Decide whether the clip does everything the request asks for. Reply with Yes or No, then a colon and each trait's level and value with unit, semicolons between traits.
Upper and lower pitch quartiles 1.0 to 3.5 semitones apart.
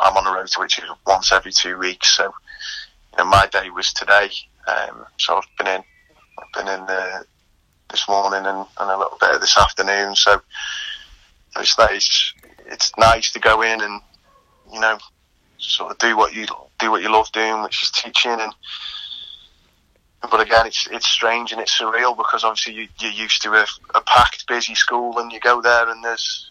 Yes: average, 2.7 semitones